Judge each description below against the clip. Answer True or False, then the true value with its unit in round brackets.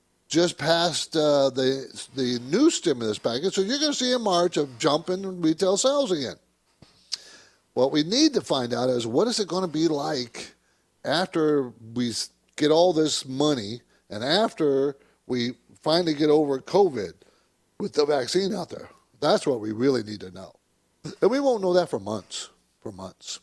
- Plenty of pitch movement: True (6.7 semitones)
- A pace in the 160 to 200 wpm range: True (180 wpm)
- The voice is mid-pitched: True (155 Hz)